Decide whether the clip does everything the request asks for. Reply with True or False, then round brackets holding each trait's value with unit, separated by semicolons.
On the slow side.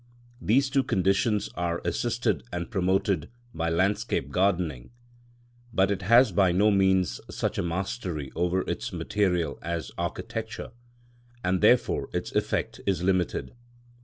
True (130 wpm)